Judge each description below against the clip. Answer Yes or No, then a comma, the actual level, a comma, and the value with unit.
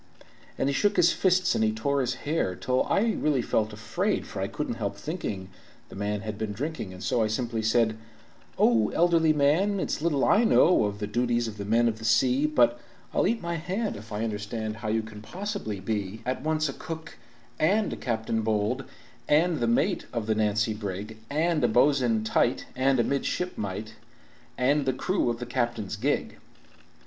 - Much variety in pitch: Yes, wide, 5.8 semitones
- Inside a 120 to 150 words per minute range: No, average, 195 wpm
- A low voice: Yes, low, 120 Hz